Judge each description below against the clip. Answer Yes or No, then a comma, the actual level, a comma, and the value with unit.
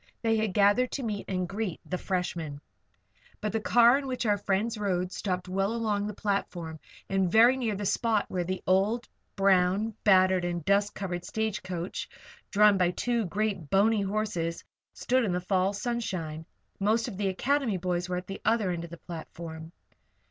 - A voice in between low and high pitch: No, high, 195 Hz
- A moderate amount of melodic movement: Yes, average, 3.3 semitones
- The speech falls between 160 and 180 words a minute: Yes, average, 175 wpm